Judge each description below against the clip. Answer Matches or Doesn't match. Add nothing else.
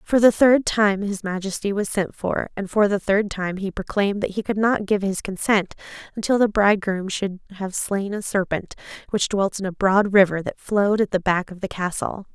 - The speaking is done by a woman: Matches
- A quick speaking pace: Matches